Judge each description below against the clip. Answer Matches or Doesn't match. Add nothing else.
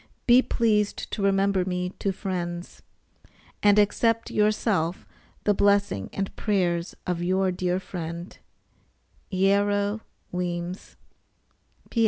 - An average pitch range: Doesn't match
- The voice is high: Matches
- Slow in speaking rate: Matches